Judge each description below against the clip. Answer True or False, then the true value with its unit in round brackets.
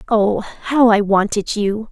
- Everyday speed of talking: True (155 wpm)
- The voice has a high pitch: True (210 Hz)